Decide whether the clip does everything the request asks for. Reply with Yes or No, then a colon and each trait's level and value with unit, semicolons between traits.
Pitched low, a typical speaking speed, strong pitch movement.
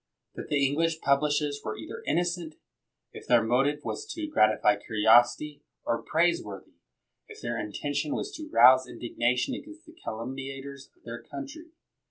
No: medium, 145 Hz; average, 145 wpm; wide, 6.0 semitones